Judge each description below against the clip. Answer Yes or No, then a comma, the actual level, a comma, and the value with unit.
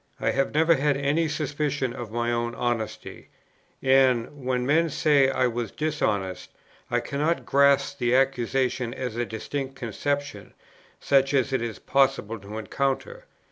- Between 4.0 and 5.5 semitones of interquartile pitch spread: No, average, 3.2 semitones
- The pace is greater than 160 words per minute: No, average, 150 wpm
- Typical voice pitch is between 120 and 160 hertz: Yes, low, 135 Hz